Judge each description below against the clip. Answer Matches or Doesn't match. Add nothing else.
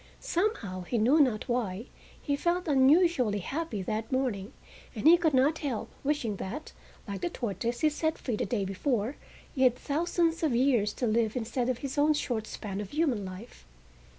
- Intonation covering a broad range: Matches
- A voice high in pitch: Matches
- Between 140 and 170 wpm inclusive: Doesn't match